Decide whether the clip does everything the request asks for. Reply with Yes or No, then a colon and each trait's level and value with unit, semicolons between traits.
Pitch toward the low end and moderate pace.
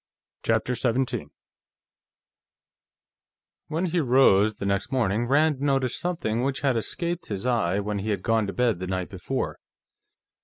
Yes: low, 120 Hz; average, 145 wpm